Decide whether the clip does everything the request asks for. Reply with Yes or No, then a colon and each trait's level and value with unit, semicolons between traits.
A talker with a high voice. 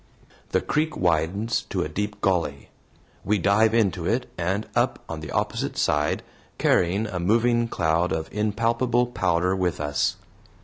No: very low, 95 Hz